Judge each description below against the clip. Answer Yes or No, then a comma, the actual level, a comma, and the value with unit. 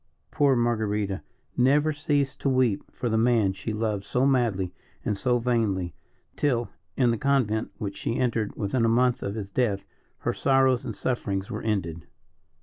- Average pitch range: Yes, average, 3.9 semitones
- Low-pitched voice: Yes, low, 115 Hz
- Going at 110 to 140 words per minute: No, average, 165 wpm